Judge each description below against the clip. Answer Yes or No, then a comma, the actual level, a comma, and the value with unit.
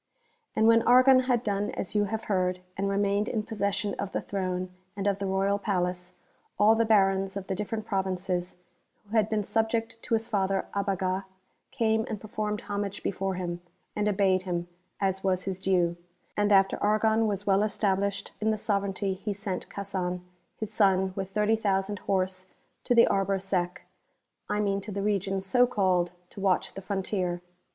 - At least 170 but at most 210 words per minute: Yes, average, 175 wpm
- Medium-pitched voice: No, high, 200 Hz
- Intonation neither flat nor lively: No, narrow, 1.8 semitones